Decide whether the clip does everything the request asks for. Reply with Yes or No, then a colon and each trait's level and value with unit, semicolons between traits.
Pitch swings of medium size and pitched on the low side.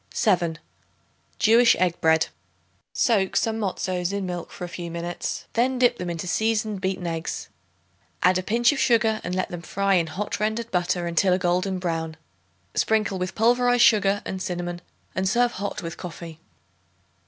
No: average, 3.9 semitones; medium, 185 Hz